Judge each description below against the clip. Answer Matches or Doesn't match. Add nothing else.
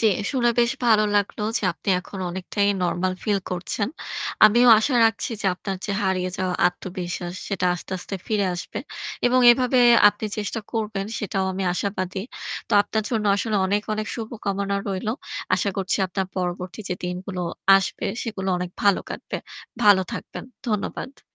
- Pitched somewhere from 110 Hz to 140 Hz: Doesn't match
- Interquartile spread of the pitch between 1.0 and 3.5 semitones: Matches